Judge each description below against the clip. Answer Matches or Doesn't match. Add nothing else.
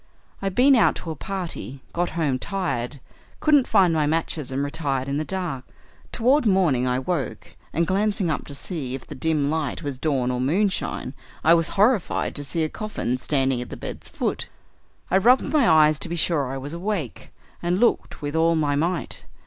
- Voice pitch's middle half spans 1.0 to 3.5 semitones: Doesn't match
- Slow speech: Doesn't match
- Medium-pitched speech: Matches